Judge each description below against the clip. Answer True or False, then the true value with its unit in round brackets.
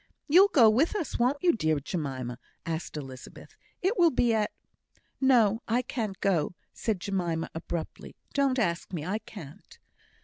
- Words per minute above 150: True (160 wpm)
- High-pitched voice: True (210 Hz)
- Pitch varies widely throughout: True (7.6 semitones)